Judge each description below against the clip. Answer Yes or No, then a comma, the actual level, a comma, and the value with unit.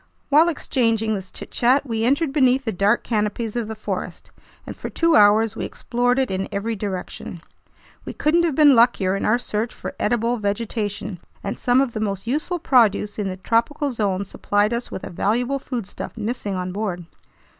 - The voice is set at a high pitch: Yes, high, 225 Hz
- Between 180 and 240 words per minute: Yes, average, 185 wpm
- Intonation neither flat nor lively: Yes, average, 3.6 semitones